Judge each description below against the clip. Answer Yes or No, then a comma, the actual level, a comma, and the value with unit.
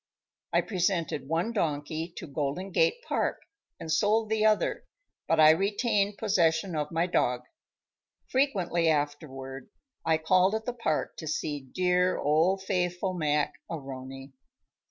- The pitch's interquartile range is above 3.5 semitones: Yes, average, 4.7 semitones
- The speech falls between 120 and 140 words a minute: Yes, slow, 135 wpm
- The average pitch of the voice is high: No, medium, 170 Hz